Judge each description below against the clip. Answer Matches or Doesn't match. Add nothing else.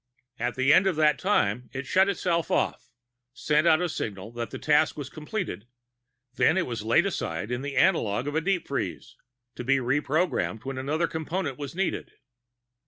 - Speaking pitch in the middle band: Matches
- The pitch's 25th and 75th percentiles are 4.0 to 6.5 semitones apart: Matches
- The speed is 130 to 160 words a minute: Doesn't match